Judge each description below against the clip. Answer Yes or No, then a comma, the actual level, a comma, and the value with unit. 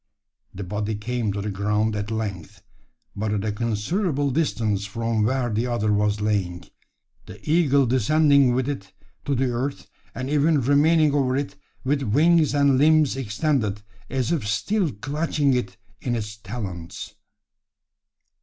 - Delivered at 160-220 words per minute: No, average, 145 wpm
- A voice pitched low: Yes, low, 120 Hz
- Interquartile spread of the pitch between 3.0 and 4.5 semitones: No, average, 5.2 semitones